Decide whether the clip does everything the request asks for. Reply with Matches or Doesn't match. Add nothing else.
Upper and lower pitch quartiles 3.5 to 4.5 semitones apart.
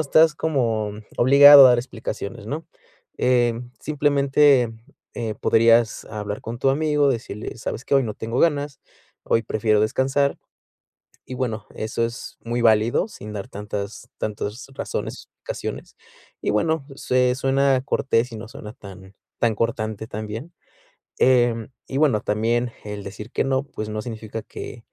Matches